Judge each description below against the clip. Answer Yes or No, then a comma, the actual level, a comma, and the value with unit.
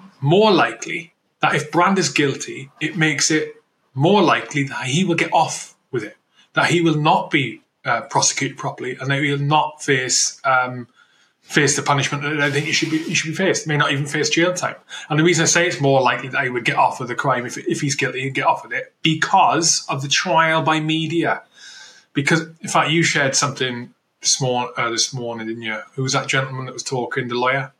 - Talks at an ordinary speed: No, fast, 230 wpm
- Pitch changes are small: No, average, 3.5 semitones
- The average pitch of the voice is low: No, medium, 145 Hz